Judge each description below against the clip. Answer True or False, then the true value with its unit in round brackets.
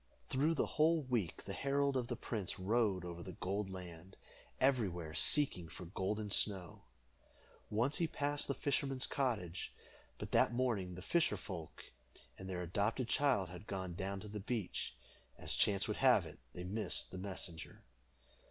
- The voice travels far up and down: True (5.9 semitones)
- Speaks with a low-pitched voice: True (100 Hz)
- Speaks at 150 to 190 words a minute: True (160 wpm)